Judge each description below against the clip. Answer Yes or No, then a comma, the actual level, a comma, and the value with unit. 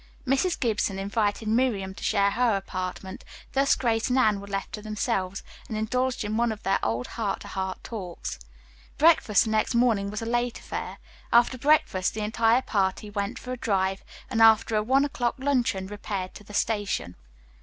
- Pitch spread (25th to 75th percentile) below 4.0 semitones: Yes, average, 3.4 semitones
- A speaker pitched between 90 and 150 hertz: No, high, 215 Hz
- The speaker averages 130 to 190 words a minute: Yes, average, 185 wpm